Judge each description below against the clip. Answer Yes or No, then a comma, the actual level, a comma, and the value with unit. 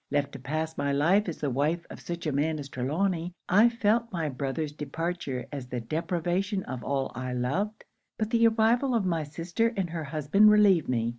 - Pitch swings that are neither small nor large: No, wide, 5.8 semitones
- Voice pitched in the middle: Yes, medium, 160 Hz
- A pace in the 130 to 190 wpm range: No, average, 200 wpm